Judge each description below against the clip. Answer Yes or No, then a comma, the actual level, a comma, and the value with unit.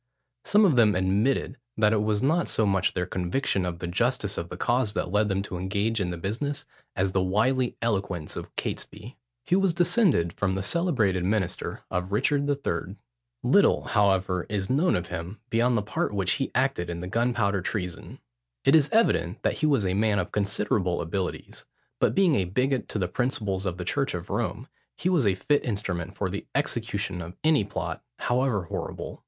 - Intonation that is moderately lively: No, wide, 5.7 semitones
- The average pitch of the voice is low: Yes, low, 105 Hz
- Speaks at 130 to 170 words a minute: No, average, 195 wpm